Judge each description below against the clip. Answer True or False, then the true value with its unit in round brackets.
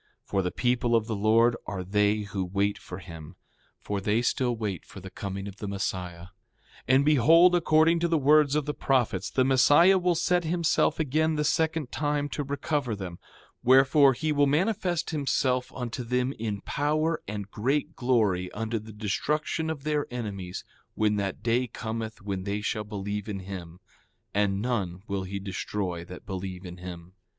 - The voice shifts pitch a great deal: True (6.7 semitones)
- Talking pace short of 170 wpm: False (175 wpm)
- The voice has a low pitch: True (115 Hz)